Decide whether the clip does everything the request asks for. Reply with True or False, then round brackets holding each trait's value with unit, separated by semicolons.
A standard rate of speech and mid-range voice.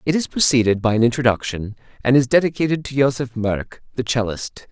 False (180 wpm; 125 Hz)